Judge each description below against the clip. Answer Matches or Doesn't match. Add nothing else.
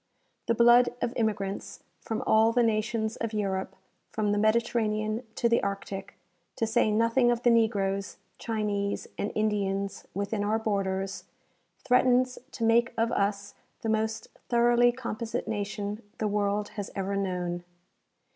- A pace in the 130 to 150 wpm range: Matches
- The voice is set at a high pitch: Matches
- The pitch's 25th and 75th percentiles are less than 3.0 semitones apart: Matches